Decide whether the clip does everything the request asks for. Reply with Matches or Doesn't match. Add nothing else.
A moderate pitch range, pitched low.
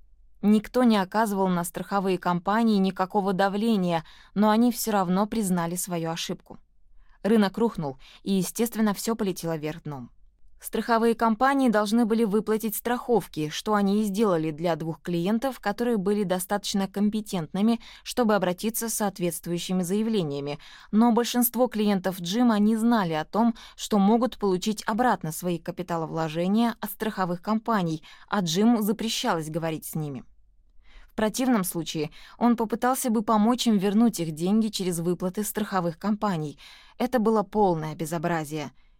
Doesn't match